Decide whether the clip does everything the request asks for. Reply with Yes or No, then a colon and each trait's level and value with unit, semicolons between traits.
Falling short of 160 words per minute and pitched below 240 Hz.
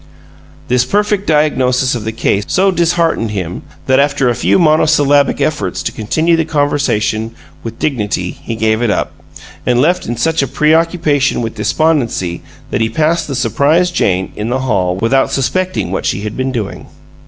No: average, 170 wpm; low, 135 Hz